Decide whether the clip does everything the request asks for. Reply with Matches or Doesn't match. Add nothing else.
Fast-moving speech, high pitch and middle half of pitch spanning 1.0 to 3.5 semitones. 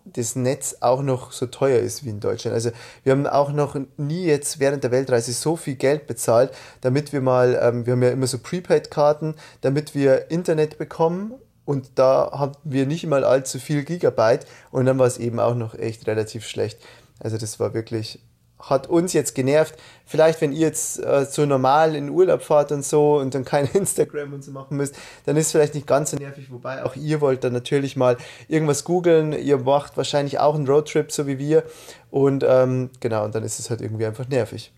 Doesn't match